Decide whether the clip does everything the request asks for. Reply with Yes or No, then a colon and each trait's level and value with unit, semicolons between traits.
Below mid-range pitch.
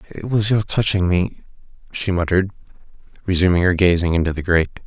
Yes: very low, 90 Hz